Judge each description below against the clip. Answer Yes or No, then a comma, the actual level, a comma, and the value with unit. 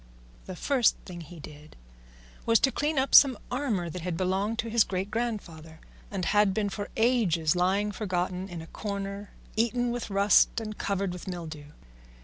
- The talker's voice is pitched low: No, high, 200 Hz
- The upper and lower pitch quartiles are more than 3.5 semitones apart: Yes, average, 4.1 semitones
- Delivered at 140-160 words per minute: No, average, 170 wpm